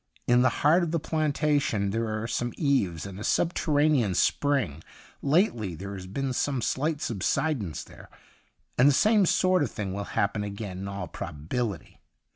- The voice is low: Yes, low, 120 Hz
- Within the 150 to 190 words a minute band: Yes, average, 165 wpm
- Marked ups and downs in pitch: Yes, wide, 6.9 semitones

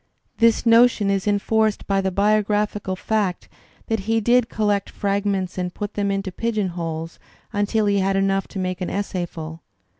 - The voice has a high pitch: Yes, high, 200 Hz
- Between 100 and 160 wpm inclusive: No, average, 170 wpm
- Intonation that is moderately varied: No, narrow, 2.1 semitones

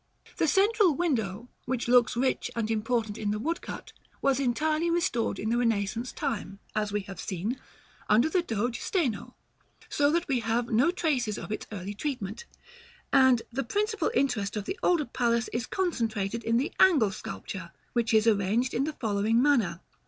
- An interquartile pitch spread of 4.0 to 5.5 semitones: Yes, average, 5.0 semitones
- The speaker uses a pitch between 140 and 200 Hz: No, high, 235 Hz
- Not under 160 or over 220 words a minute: Yes, average, 170 wpm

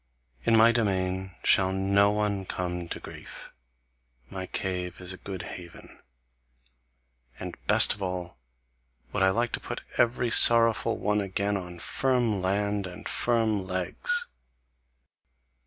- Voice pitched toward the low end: Yes, low, 100 Hz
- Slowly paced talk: Yes, slow, 130 wpm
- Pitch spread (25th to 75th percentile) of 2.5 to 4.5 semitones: Yes, average, 3.2 semitones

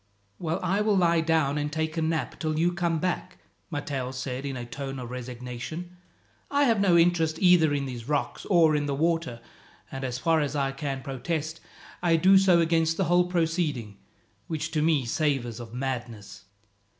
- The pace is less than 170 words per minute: No, average, 185 wpm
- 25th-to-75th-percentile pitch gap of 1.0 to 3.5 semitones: No, average, 4.1 semitones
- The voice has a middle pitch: Yes, medium, 155 Hz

